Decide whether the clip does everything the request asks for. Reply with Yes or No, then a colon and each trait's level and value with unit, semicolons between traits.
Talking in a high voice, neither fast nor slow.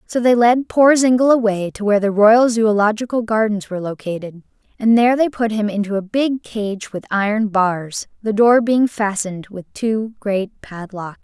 Yes: high, 215 Hz; average, 180 wpm